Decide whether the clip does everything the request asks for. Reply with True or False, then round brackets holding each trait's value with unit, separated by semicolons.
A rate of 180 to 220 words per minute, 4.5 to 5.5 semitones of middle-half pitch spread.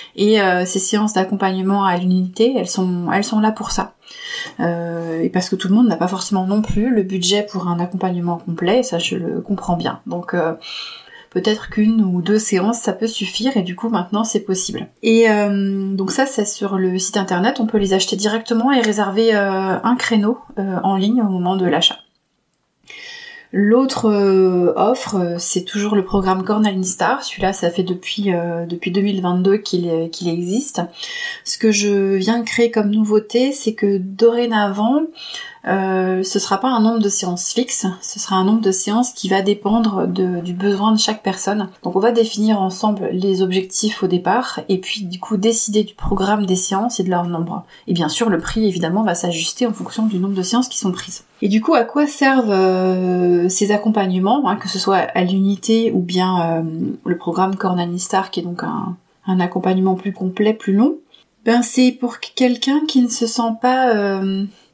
False (200 wpm; 3.2 semitones)